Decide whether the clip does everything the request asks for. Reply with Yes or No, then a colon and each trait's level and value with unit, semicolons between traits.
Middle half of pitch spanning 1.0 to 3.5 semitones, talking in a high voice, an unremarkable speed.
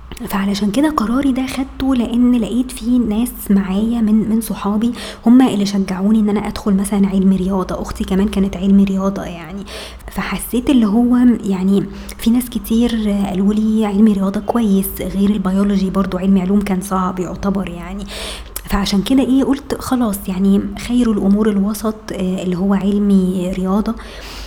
No: narrow, 2.6 semitones; high, 205 Hz; fast, 150 wpm